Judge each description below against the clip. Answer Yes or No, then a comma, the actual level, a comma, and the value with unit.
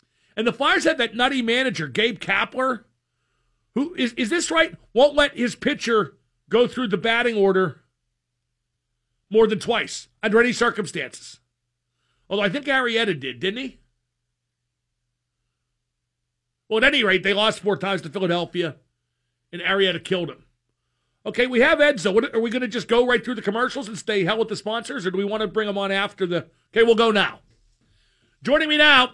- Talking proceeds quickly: No, average, 180 wpm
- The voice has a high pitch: Yes, high, 205 Hz